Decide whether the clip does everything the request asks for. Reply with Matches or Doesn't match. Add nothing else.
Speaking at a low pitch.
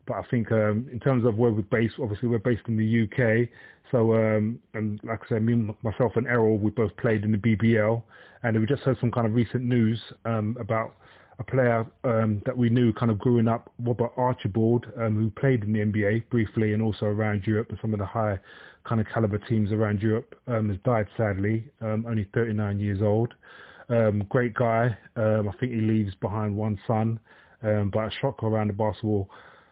Matches